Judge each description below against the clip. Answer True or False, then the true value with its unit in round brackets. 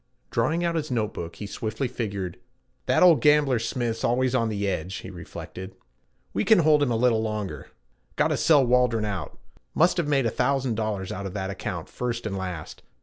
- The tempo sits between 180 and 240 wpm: True (195 wpm)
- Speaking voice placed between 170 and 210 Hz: False (115 Hz)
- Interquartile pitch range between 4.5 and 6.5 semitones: True (5.1 semitones)